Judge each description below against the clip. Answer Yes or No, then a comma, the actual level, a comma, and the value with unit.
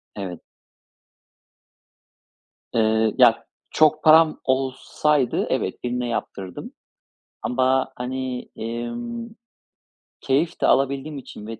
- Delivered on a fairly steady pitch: No, average, 4.4 semitones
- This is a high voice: No, low, 130 Hz